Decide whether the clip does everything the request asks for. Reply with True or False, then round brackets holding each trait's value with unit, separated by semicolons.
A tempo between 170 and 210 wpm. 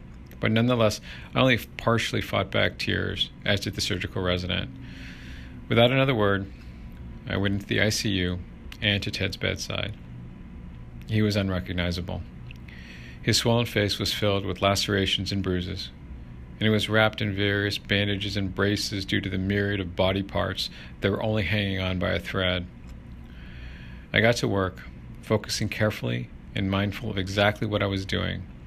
False (155 wpm)